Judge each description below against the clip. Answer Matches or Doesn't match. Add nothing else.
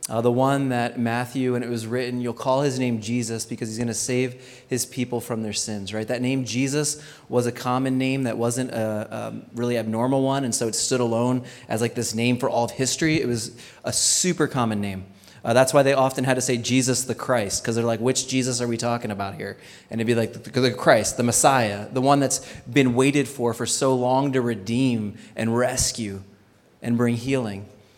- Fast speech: Matches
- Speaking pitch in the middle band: Doesn't match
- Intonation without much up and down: Matches